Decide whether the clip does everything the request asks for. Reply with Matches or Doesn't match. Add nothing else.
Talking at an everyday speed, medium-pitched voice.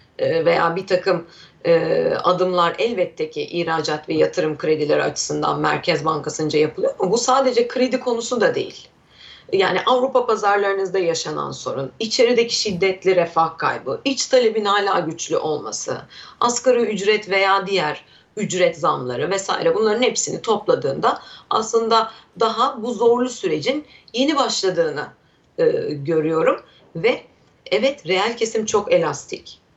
Doesn't match